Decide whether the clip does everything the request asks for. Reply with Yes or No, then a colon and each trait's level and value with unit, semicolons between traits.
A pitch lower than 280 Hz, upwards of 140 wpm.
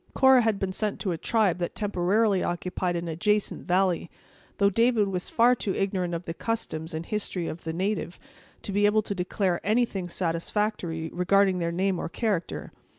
Yes: high, 190 Hz; average, 180 wpm